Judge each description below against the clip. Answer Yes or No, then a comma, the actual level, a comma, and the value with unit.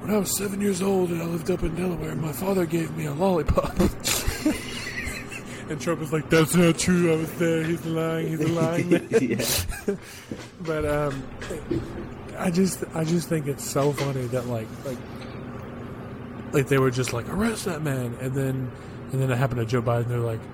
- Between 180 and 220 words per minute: Yes, average, 185 wpm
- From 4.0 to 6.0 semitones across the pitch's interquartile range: Yes, average, 5.2 semitones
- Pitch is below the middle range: No, medium, 145 Hz